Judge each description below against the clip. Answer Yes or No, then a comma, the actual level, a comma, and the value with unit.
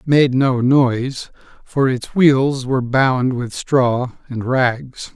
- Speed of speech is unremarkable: Yes, average, 150 wpm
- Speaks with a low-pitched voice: Yes, low, 130 Hz